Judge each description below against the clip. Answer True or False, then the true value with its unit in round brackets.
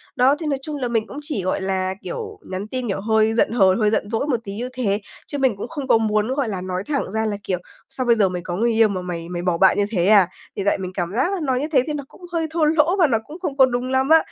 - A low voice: False (225 Hz)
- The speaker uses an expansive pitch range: True (6.0 semitones)